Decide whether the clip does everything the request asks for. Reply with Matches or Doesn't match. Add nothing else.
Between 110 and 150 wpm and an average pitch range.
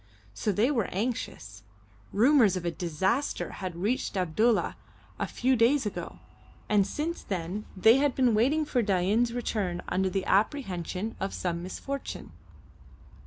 Matches